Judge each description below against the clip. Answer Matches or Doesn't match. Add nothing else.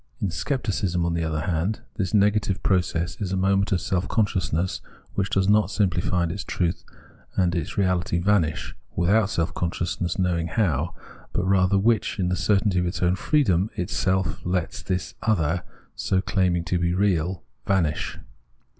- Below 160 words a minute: Doesn't match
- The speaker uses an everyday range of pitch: Doesn't match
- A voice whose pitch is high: Doesn't match